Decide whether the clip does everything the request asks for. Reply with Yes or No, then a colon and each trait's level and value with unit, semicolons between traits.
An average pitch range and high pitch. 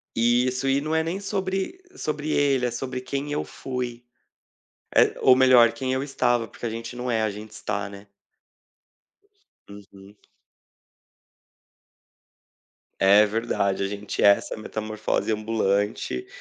No: average, 4.0 semitones; low, 120 Hz